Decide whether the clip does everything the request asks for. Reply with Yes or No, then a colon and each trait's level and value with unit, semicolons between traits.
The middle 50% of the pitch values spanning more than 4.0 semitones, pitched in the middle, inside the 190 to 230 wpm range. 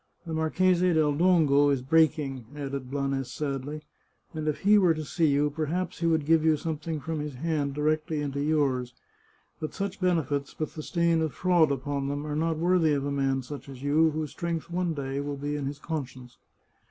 No: narrow, 2.5 semitones; medium, 150 Hz; average, 200 wpm